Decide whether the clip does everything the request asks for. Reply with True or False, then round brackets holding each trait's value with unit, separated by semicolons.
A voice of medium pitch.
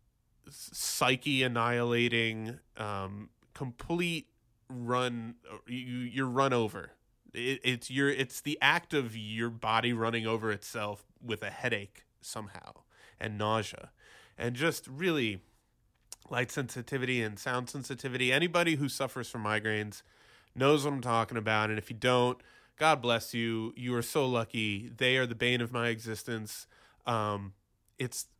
False (120 Hz)